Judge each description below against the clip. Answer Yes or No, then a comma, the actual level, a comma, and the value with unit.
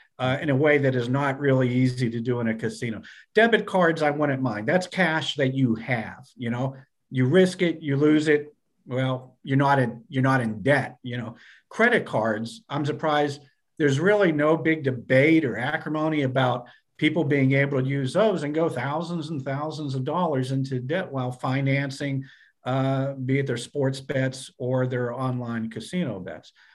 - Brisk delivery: No, average, 185 wpm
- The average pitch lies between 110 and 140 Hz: Yes, low, 135 Hz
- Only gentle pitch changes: No, average, 3.0 semitones